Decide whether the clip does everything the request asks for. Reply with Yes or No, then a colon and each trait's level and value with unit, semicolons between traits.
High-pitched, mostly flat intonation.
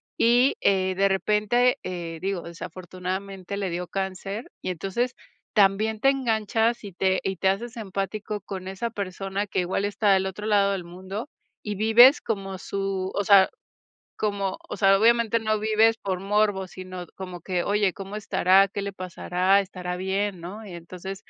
Yes: high, 195 Hz; narrow, 2.1 semitones